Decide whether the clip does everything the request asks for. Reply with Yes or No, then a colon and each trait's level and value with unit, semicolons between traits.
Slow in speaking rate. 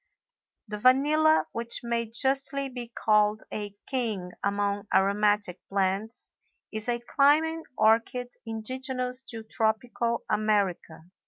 Yes: slow, 105 wpm